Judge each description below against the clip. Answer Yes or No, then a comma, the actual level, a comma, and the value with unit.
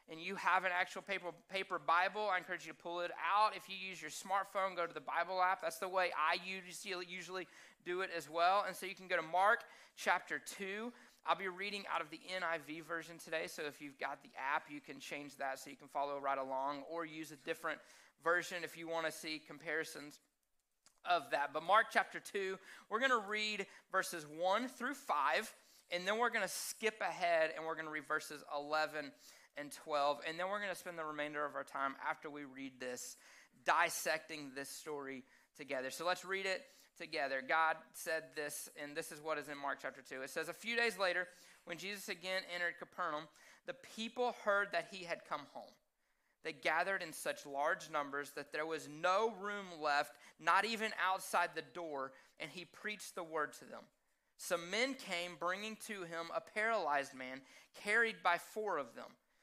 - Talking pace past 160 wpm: Yes, fast, 205 wpm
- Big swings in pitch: No, average, 4.0 semitones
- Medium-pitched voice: Yes, medium, 170 Hz